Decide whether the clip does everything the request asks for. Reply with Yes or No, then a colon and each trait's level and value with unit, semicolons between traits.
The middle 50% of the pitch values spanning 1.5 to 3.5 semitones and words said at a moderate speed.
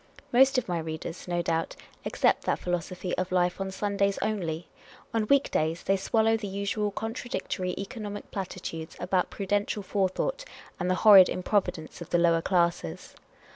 Yes: average, 3.0 semitones; average, 160 wpm